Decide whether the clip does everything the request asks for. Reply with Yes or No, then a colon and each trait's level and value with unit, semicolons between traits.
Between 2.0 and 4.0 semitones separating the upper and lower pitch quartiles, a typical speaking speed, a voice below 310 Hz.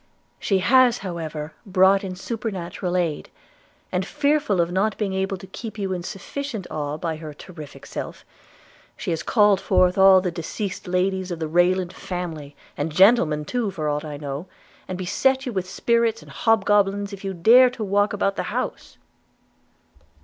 Yes: average, 3.3 semitones; average, 170 wpm; high, 190 Hz